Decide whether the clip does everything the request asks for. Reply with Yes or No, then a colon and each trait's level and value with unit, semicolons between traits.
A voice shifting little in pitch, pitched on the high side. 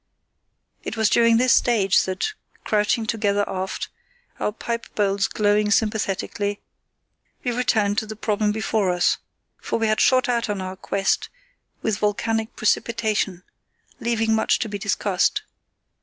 Yes: narrow, 1.9 semitones; high, 215 Hz